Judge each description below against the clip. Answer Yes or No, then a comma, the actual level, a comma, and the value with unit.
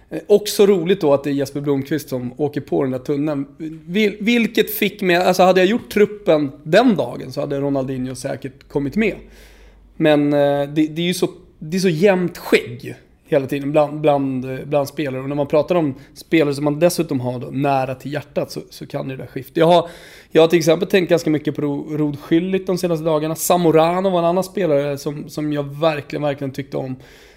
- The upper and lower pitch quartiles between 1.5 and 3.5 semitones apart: No, average, 3.9 semitones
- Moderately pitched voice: Yes, medium, 150 Hz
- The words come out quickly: Yes, fast, 210 wpm